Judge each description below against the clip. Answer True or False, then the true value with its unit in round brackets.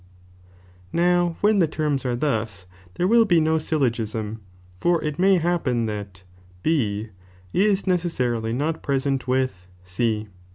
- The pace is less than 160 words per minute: True (135 wpm)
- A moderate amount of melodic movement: False (7.4 semitones)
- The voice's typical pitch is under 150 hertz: True (140 Hz)